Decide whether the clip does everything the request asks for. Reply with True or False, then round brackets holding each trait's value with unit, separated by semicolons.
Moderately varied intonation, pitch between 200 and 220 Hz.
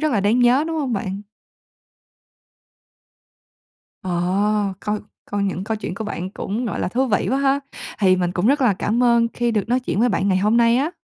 True (3.9 semitones; 215 Hz)